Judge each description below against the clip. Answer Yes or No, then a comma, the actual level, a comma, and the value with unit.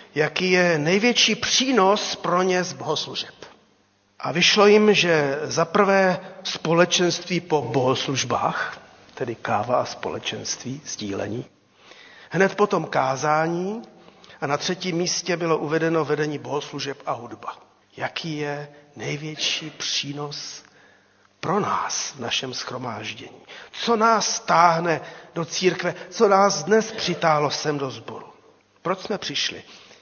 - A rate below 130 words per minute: Yes, average, 120 wpm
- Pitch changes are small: No, average, 3.9 semitones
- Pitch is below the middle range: No, medium, 170 Hz